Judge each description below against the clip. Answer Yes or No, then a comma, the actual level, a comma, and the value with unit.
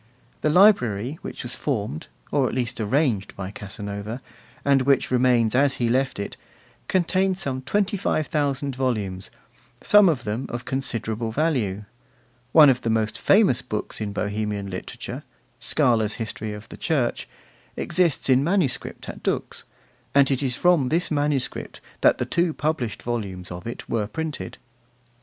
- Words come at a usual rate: Yes, average, 145 wpm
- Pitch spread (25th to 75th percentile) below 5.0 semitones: No, wide, 5.6 semitones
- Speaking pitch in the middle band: No, low, 125 Hz